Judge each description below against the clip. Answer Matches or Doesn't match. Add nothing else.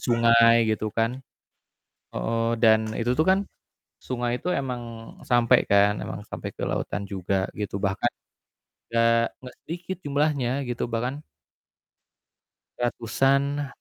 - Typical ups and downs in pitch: Matches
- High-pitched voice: Doesn't match